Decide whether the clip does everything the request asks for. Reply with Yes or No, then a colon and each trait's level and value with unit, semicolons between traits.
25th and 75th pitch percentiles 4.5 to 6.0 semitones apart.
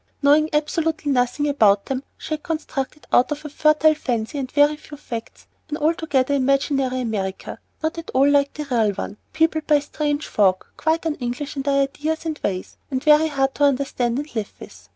No: average, 3.0 semitones